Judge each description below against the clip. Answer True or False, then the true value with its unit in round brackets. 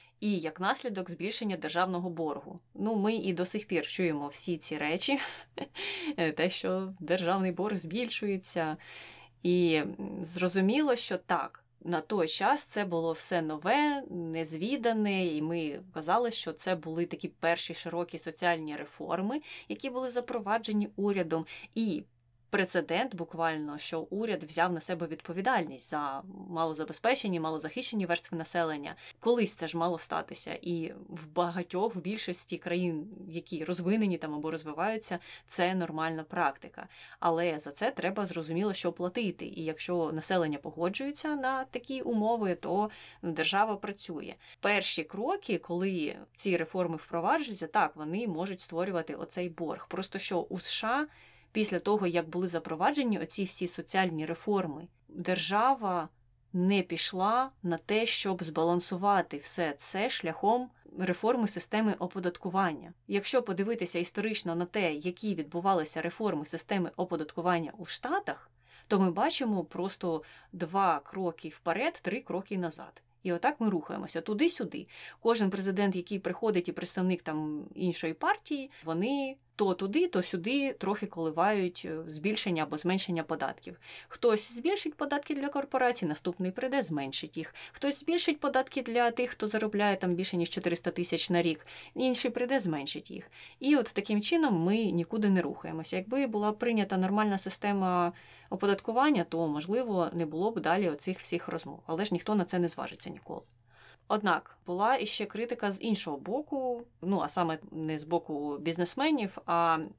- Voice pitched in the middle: True (180 Hz)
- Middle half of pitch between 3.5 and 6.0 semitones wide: True (4.1 semitones)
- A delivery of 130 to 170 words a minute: True (140 wpm)